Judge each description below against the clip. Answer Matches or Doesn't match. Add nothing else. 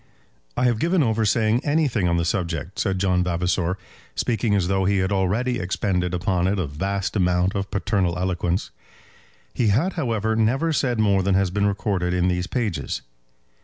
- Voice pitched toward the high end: Doesn't match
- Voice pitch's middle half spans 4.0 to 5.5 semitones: Doesn't match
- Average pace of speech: Matches